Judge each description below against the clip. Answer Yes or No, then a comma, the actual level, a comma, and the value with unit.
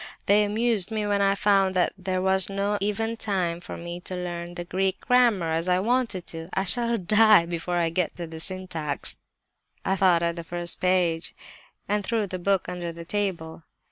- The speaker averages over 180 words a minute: Yes, average, 195 wpm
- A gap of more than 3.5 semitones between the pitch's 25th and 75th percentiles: No, average, 3.0 semitones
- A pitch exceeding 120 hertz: Yes, medium, 185 Hz